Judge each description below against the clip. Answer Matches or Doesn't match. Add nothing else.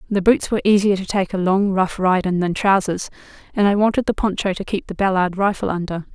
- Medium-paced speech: Doesn't match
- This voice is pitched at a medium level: Doesn't match